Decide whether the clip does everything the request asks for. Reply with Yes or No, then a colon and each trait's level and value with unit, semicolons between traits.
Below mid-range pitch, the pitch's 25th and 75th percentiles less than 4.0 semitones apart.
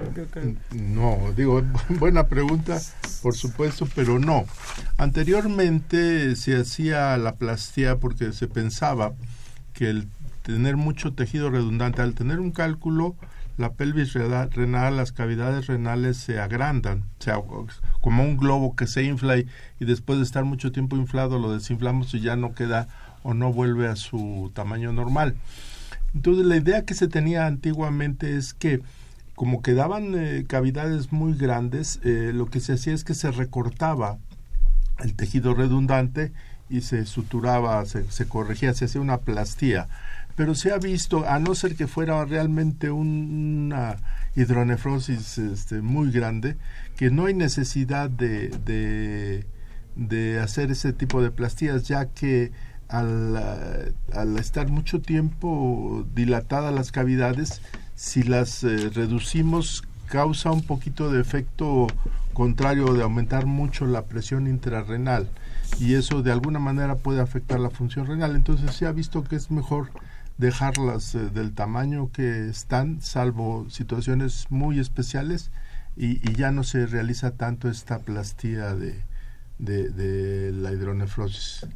Yes: low, 125 Hz; average, 3.4 semitones